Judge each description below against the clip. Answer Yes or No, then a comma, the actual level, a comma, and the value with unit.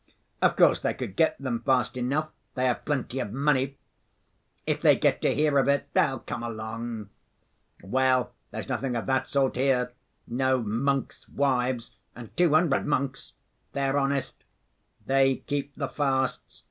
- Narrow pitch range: Yes, narrow, 2.1 semitones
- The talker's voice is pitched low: Yes, low, 130 Hz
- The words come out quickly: No, average, 155 wpm